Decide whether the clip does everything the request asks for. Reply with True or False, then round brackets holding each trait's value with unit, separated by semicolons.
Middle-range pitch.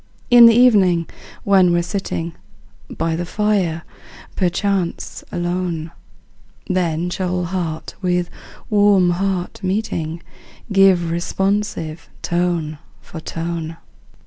True (175 Hz)